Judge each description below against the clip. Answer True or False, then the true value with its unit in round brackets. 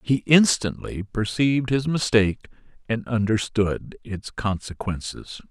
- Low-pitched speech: True (115 Hz)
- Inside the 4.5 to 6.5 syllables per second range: False (4.3 syllables/s)